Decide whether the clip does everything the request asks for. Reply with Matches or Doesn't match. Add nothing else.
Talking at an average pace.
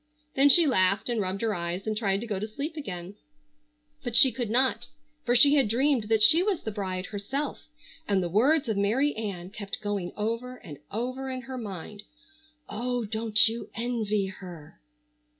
Matches